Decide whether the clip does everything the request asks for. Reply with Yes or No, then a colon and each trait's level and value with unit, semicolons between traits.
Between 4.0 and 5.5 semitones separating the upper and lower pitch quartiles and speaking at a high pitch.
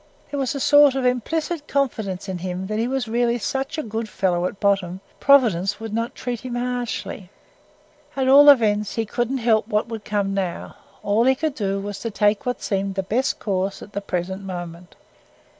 Yes: average, 4.3 semitones; high, 220 Hz